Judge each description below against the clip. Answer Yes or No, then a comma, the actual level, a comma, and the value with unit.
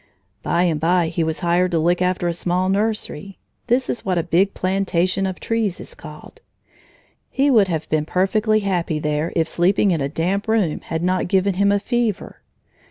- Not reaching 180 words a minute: No, average, 190 wpm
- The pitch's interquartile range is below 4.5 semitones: Yes, average, 3.0 semitones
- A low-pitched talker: No, medium, 185 Hz